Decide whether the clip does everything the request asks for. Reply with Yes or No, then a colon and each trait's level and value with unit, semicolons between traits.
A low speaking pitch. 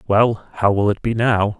Yes: low, 105 Hz